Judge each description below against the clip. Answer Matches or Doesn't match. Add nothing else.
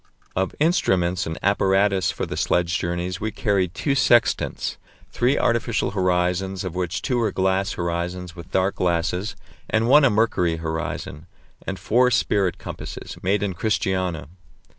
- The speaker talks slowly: Doesn't match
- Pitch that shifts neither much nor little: Matches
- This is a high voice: Doesn't match